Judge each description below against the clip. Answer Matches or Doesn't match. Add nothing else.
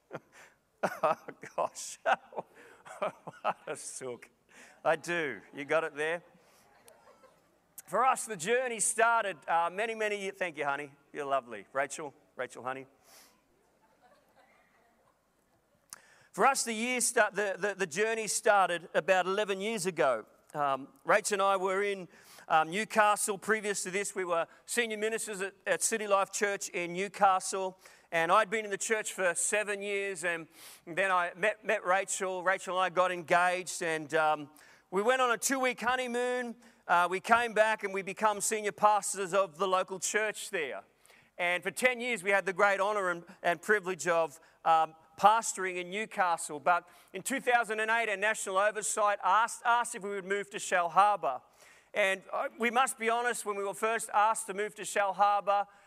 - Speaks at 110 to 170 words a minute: Matches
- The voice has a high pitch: Matches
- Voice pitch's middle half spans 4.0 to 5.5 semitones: Doesn't match